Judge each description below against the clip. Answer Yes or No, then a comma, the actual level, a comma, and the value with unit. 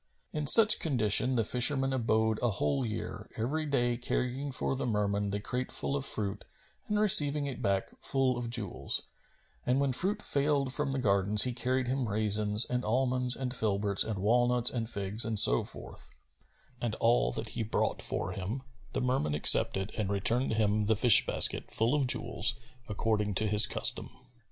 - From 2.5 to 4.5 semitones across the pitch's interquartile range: Yes, average, 4.0 semitones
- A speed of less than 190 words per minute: Yes, average, 175 wpm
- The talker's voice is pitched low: Yes, low, 120 Hz